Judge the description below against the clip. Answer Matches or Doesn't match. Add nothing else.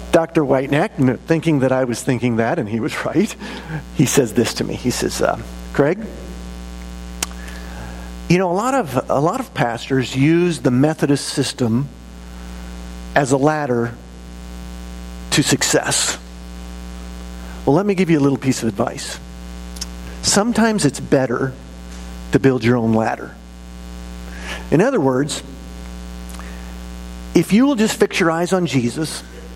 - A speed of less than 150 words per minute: Matches